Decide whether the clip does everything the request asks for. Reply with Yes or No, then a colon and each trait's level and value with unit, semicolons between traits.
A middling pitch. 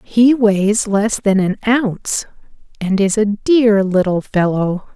No: high, 205 Hz